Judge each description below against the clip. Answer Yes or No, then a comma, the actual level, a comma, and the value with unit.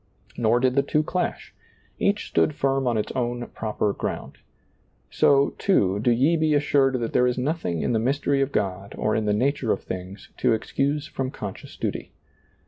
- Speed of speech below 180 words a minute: No, average, 185 wpm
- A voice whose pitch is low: Yes, low, 125 Hz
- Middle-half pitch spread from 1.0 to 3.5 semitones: No, average, 4.5 semitones